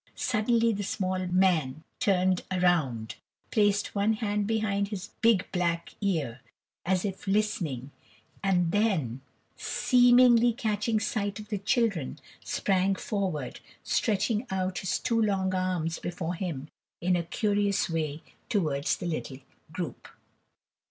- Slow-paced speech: Yes, slow, 125 wpm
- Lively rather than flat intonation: No, average, 3.8 semitones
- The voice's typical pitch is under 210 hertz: Yes, high, 190 Hz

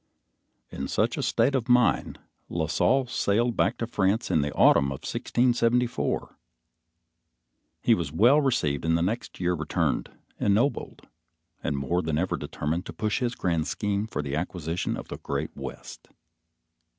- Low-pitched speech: Yes, very low, 95 Hz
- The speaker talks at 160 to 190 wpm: No, average, 150 wpm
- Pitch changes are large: Yes, wide, 6.9 semitones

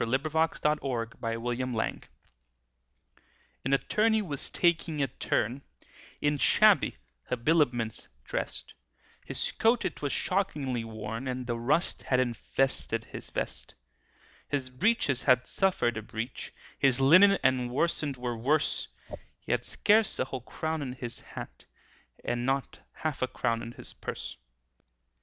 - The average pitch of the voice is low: Yes, low, 130 Hz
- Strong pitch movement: No, average, 4.3 semitones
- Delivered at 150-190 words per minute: No, slow, 135 wpm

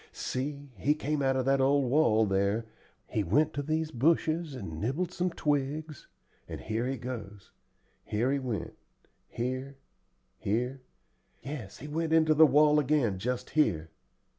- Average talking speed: Yes, average, 150 wpm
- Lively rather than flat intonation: No, average, 4.5 semitones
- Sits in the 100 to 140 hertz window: Yes, low, 135 Hz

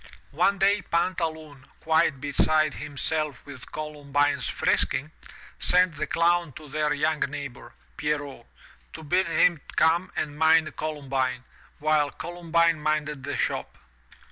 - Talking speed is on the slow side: Yes, slow, 120 wpm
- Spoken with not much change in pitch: Yes, narrow, 2.3 semitones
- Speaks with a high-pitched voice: No, medium, 155 Hz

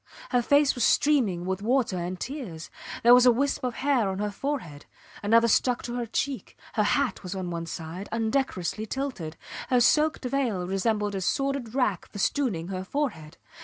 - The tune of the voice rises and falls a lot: Yes, wide, 6.1 semitones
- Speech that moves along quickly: No, average, 175 wpm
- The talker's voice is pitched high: Yes, high, 225 Hz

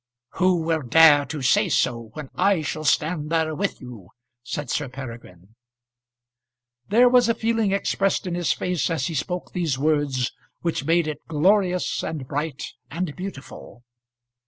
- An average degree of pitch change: Yes, average, 5.0 semitones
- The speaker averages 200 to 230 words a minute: No, average, 155 wpm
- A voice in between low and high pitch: Yes, medium, 155 Hz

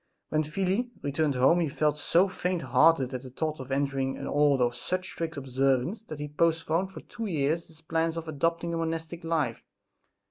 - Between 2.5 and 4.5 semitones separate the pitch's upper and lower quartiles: Yes, average, 3.3 semitones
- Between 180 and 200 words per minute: Yes, average, 190 wpm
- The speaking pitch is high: No, medium, 155 Hz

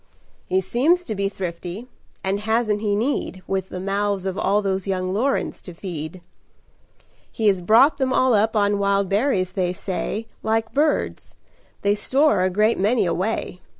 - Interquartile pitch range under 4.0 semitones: Yes, average, 3.1 semitones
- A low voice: No, high, 200 Hz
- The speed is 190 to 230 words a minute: No, average, 165 wpm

